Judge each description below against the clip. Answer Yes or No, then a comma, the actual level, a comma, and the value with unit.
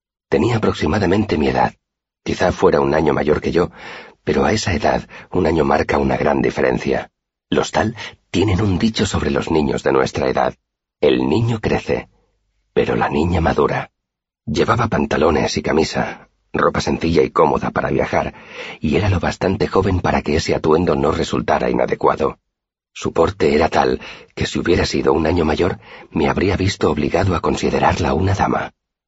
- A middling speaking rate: Yes, average, 165 wpm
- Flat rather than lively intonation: No, average, 3.4 semitones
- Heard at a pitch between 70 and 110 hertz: Yes, very low, 95 Hz